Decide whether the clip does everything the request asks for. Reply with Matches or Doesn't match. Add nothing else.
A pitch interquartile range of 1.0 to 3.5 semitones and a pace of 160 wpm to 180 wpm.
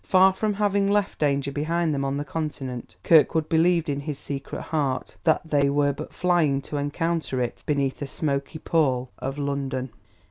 Matches